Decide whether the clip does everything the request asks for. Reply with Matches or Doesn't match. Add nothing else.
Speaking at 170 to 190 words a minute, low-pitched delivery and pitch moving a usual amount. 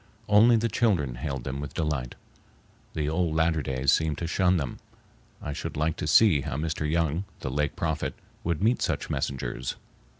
Matches